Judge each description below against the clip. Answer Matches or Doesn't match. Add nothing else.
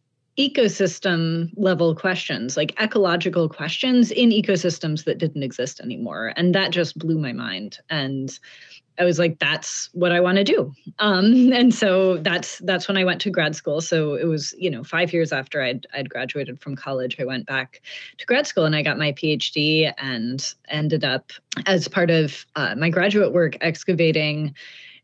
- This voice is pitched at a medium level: Matches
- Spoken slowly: Doesn't match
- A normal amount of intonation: Matches